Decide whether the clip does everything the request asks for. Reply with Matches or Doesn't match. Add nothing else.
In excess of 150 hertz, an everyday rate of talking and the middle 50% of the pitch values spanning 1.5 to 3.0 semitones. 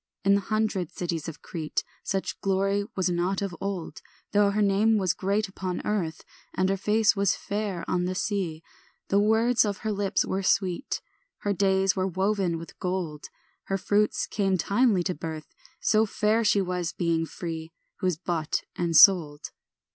Matches